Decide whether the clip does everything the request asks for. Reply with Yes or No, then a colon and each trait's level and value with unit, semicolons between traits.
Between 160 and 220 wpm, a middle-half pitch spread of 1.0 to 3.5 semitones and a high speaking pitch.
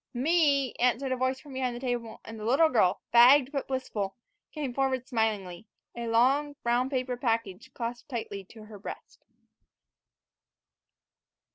No: average, 145 wpm; average, 2.9 semitones; high, 245 Hz